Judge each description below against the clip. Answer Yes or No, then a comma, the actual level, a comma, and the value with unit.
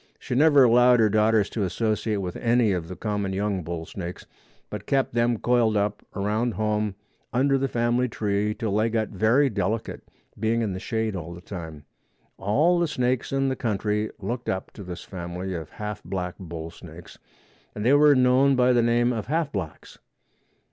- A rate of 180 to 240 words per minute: Yes, average, 185 wpm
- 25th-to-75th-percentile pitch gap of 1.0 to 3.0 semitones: No, average, 4.1 semitones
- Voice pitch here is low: Yes, low, 110 Hz